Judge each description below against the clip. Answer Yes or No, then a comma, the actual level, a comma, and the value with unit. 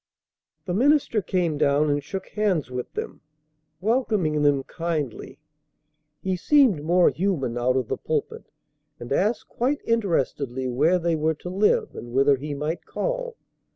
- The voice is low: No, medium, 165 Hz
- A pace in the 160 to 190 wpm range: No, average, 150 wpm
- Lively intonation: Yes, wide, 6.3 semitones